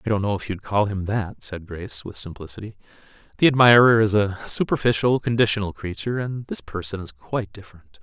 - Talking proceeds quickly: No, average, 195 wpm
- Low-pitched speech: Yes, low, 105 Hz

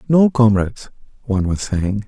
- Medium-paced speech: Yes, average, 145 wpm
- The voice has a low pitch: Yes, low, 110 Hz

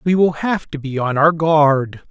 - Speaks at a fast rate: Yes, fast, 230 wpm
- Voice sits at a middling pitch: Yes, medium, 155 Hz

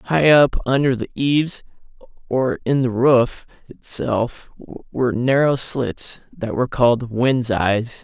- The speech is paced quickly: No, slow, 135 wpm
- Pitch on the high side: No, low, 125 Hz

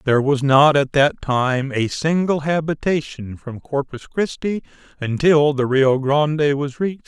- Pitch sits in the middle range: Yes, medium, 145 Hz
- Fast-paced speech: No, average, 155 wpm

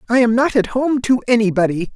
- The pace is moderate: No, fast, 215 wpm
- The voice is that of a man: Yes, male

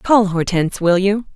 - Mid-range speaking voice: No, high, 195 Hz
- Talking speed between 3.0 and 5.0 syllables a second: Yes, 4.8 syllables/s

